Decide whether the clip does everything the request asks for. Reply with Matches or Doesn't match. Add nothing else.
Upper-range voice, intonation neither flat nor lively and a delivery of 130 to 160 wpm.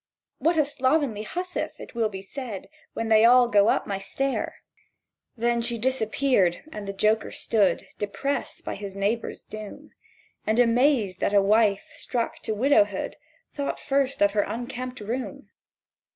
Matches